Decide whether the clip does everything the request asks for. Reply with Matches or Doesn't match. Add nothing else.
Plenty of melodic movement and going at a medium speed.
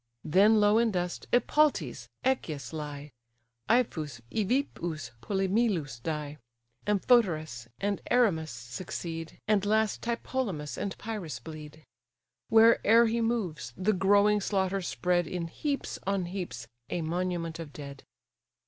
Doesn't match